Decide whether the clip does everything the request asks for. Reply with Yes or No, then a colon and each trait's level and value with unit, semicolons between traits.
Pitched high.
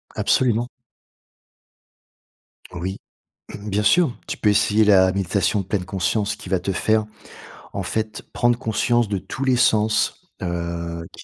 No: low, 105 Hz